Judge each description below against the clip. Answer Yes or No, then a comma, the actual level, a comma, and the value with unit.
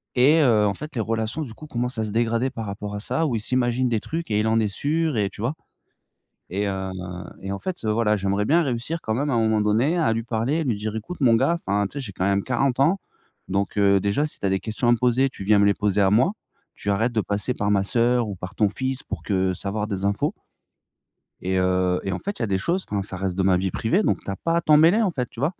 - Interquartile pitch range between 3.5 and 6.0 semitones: Yes, average, 4.7 semitones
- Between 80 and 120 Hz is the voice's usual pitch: Yes, low, 110 Hz